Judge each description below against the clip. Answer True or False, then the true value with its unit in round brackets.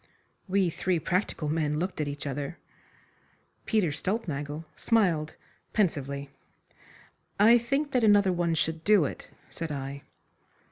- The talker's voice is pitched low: False (165 Hz)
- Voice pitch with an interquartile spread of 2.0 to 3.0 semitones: False (5.4 semitones)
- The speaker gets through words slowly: True (125 wpm)